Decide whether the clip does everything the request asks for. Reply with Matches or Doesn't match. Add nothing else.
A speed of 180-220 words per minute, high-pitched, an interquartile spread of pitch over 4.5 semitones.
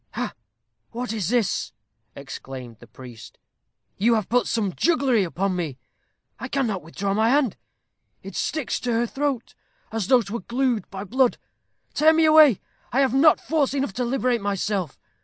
Doesn't match